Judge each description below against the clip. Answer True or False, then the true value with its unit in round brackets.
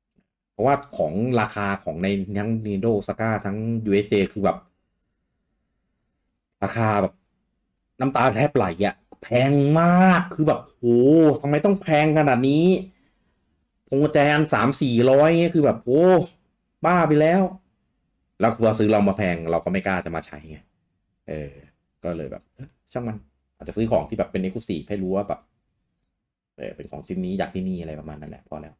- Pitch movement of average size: False (8.2 semitones)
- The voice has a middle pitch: False (110 Hz)